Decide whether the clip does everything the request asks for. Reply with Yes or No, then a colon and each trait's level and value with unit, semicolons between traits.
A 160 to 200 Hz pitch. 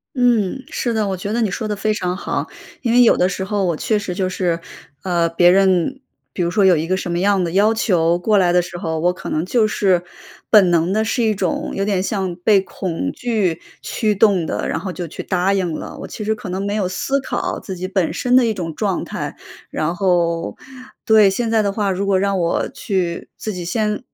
Yes: high, 190 Hz